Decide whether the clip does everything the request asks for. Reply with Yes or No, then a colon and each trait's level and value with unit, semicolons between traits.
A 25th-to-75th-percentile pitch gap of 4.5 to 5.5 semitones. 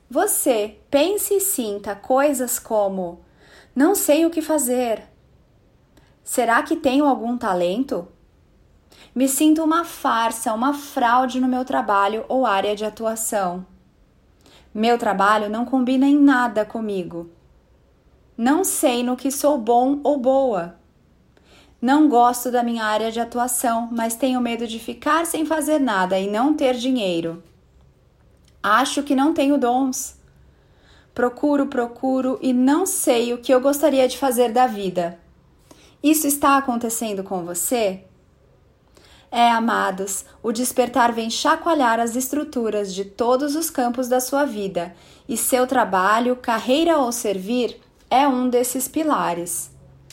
No: average, 3.8 semitones